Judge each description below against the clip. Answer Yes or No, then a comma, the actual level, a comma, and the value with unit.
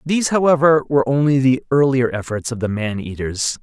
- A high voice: No, low, 130 Hz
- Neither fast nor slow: Yes, average, 180 wpm